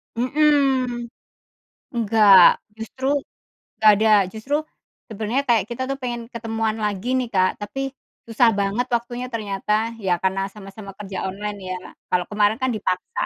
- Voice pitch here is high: Yes, high, 220 Hz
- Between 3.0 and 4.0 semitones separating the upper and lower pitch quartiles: Yes, average, 3.3 semitones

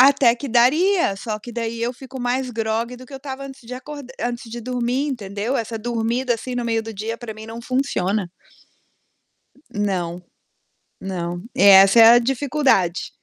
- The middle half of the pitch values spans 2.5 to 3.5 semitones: Yes, average, 3.0 semitones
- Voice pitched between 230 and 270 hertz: Yes, high, 235 Hz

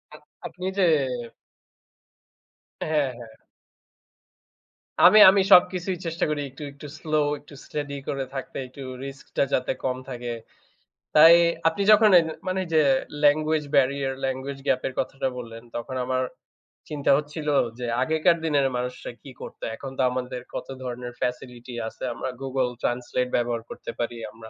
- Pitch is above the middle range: No, low, 135 Hz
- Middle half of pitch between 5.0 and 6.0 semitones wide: No, average, 3.4 semitones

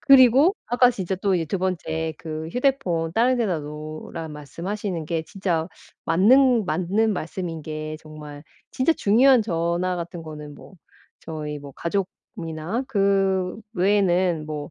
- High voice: No, medium, 175 Hz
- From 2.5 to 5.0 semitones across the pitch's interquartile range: Yes, average, 4.6 semitones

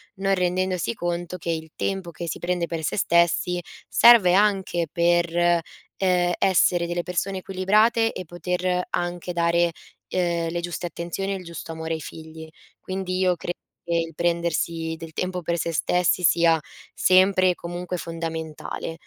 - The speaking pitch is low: No, medium, 175 Hz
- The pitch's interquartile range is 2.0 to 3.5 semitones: No, narrow, 1.5 semitones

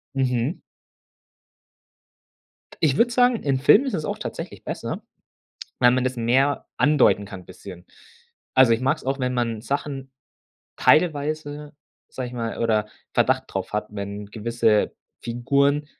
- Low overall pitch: Yes, low, 130 Hz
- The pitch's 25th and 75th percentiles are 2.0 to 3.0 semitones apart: No, average, 4.1 semitones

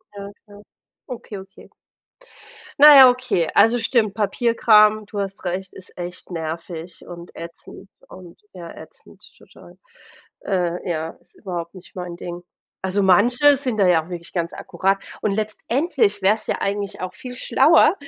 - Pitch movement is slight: No, average, 4.0 semitones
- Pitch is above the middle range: Yes, high, 195 Hz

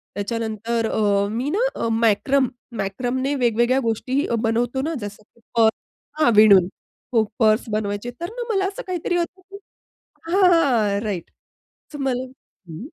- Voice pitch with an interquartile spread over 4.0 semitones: Yes, average, 4.9 semitones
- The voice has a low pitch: No, high, 235 Hz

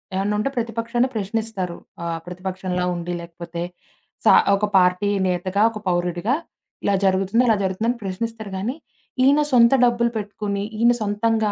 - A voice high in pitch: Yes, high, 205 Hz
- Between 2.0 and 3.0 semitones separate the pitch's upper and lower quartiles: No, average, 3.8 semitones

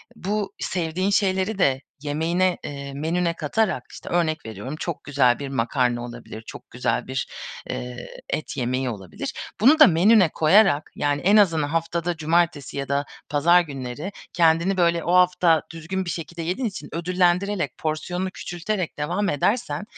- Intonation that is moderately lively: Yes, average, 4.2 semitones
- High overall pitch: No, medium, 165 Hz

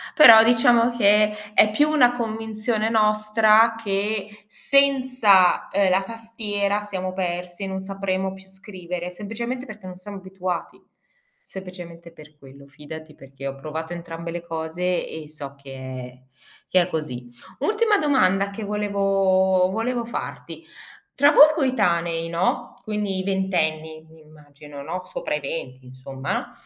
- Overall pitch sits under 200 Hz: Yes, high, 190 Hz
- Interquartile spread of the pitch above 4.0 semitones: Yes, average, 4.6 semitones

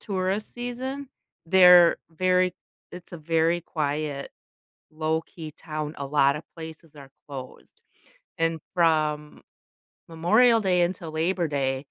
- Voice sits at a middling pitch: Yes, medium, 165 Hz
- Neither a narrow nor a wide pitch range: Yes, average, 3.1 semitones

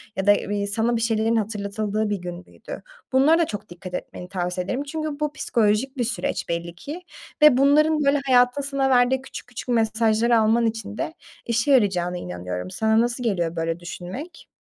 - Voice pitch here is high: Yes, high, 225 Hz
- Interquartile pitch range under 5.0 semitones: No, wide, 5.5 semitones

